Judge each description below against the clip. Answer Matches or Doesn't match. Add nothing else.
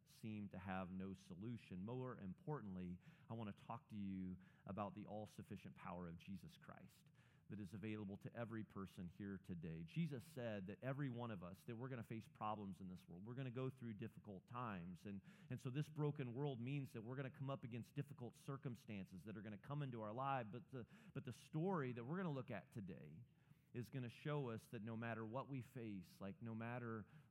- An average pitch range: Matches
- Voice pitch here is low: Matches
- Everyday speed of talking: Doesn't match